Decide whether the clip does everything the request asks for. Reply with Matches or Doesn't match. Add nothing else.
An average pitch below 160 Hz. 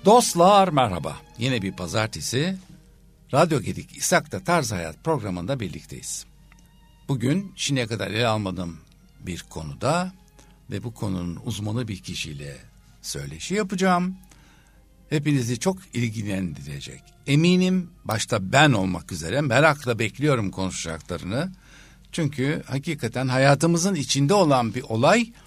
Matches